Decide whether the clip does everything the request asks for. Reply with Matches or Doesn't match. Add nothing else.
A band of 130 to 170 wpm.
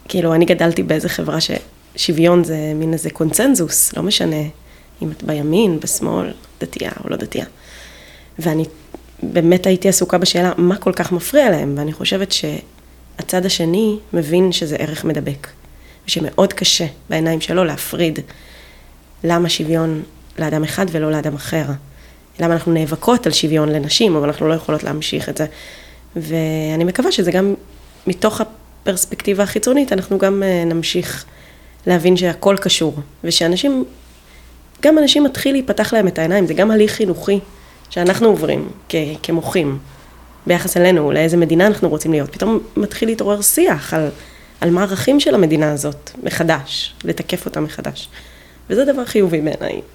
Matches